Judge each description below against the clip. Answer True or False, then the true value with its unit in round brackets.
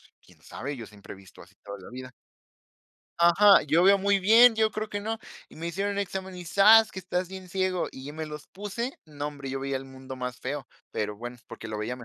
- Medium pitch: True (165 Hz)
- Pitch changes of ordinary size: False (7.2 semitones)